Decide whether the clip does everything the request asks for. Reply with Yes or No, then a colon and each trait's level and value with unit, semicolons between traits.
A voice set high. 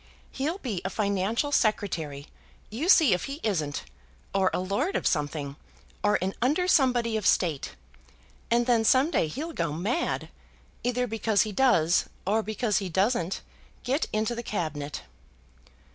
Yes: high, 215 Hz